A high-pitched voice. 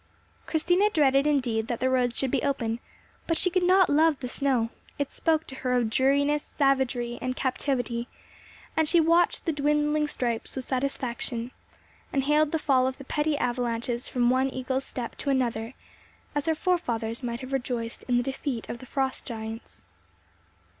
Yes: very high, 265 Hz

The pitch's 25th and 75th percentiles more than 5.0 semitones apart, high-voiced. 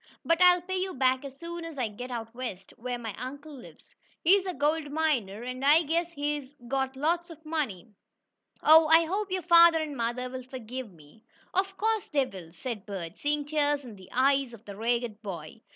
Yes: wide, 5.4 semitones; very high, 275 Hz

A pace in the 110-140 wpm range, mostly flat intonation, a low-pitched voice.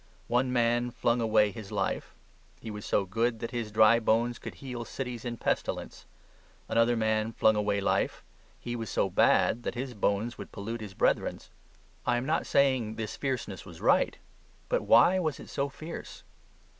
No: average, 175 wpm; narrow, 2.1 semitones; low, 115 Hz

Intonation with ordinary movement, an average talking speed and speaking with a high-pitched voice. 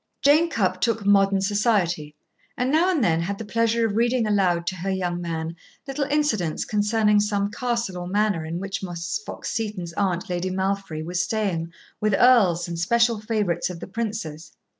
Yes: average, 4.4 semitones; average, 180 wpm; high, 200 Hz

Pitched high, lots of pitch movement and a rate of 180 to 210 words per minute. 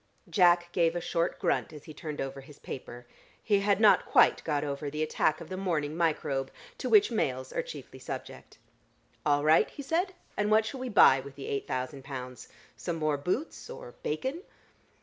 No: medium, 160 Hz; wide, 7.0 semitones; average, 190 wpm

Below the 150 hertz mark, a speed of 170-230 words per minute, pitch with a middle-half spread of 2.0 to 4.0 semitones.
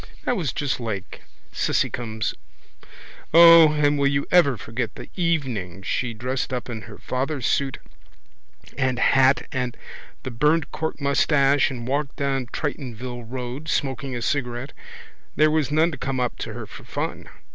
No: low, 135 Hz; average, 155 wpm; average, 3.2 semitones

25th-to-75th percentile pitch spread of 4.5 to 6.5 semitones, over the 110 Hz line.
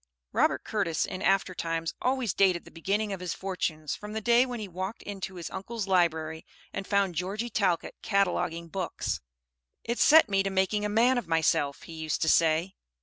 No: average, 3.8 semitones; high, 190 Hz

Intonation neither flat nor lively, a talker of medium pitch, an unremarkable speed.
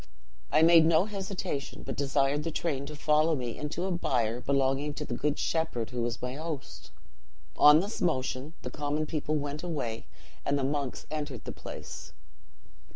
Yes: average, 3.2 semitones; medium, 150 Hz; average, 170 wpm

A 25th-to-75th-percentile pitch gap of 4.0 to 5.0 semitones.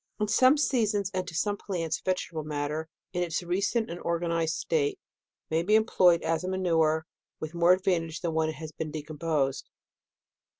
No: average, 2.9 semitones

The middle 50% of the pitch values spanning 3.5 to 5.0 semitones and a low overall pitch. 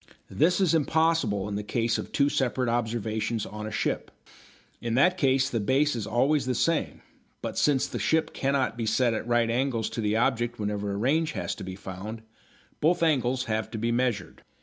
Yes: average, 4.1 semitones; low, 120 Hz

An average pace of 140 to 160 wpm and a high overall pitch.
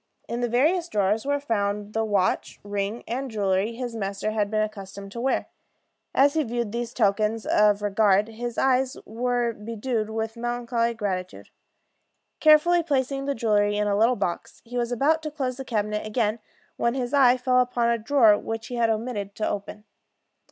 No: average, 180 wpm; high, 230 Hz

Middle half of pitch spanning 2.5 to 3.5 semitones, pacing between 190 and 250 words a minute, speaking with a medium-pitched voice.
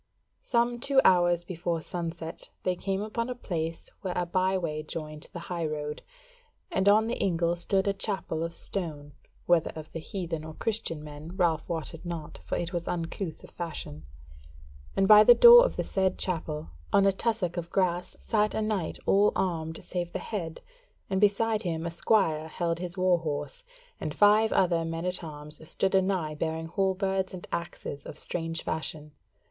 No: average, 3.2 semitones; average, 175 wpm; medium, 175 Hz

